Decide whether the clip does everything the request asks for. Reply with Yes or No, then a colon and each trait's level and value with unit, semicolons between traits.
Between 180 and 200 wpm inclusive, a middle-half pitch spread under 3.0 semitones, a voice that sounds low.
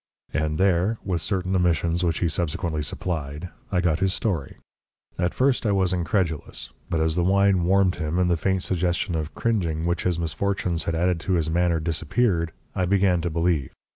Yes: average, 185 wpm; narrow, 2.5 semitones; very low, 90 Hz